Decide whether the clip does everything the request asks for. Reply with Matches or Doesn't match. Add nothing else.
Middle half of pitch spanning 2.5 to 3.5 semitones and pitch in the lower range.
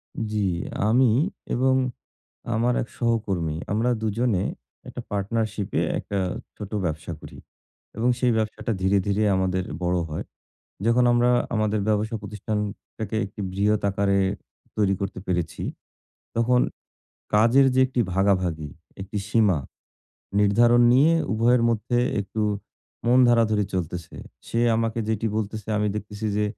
Matches